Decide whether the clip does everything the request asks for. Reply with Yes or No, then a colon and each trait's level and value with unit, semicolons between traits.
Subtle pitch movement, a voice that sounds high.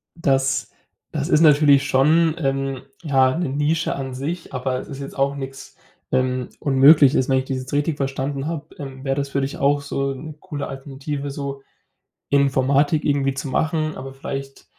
No: narrow, 1.4 semitones; medium, 140 Hz